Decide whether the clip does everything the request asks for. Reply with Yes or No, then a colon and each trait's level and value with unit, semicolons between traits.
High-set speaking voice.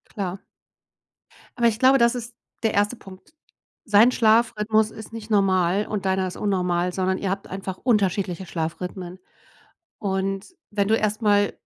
Yes: high, 200 Hz